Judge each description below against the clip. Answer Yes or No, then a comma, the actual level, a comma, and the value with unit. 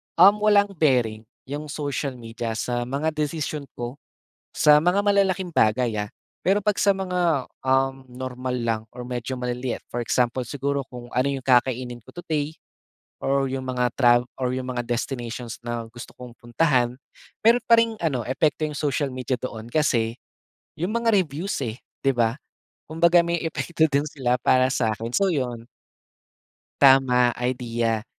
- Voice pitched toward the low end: Yes, low, 130 Hz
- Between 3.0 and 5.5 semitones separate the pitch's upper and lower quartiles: Yes, average, 4.2 semitones